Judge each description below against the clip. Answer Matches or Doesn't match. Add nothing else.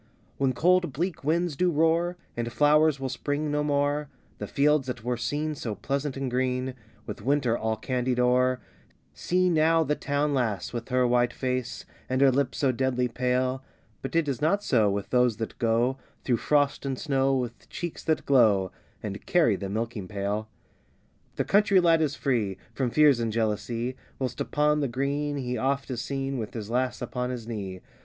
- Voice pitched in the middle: Doesn't match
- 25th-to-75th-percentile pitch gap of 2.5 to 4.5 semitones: Matches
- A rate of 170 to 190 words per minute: Matches